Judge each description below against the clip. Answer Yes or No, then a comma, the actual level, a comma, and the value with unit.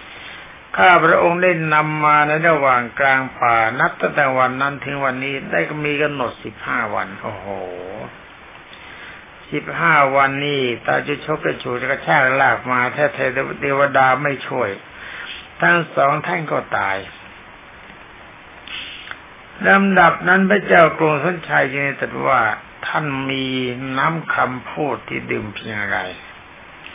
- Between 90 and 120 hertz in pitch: No, medium, 140 Hz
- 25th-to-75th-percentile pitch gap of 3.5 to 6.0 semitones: No, average, 3.0 semitones